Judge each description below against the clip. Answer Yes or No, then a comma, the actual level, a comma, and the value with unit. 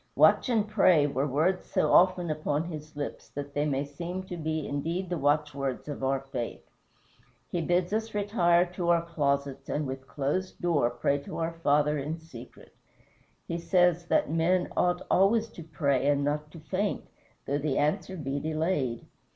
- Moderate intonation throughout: Yes, average, 3.7 semitones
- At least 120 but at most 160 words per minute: No, average, 175 wpm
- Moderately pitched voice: Yes, medium, 155 Hz